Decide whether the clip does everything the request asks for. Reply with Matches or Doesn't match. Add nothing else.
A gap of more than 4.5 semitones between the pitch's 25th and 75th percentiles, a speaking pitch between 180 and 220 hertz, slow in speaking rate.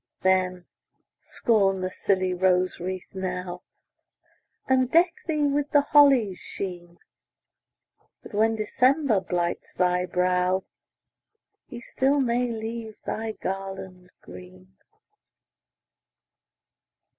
Matches